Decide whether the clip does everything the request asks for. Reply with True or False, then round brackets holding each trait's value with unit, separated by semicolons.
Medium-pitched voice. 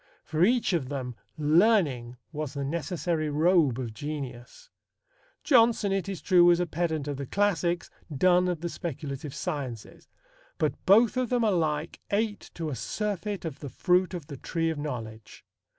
True (165 Hz)